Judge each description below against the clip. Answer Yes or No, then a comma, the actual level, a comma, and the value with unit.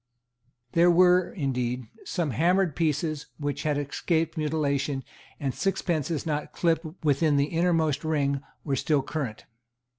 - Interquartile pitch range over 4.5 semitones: No, average, 2.9 semitones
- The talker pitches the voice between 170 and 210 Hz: No, medium, 155 Hz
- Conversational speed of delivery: No, slow, 125 wpm